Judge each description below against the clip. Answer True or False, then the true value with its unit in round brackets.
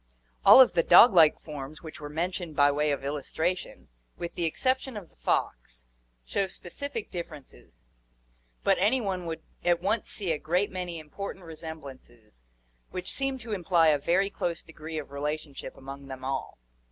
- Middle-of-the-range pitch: True (165 Hz)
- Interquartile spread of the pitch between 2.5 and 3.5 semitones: False (4.3 semitones)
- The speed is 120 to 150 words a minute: False (165 wpm)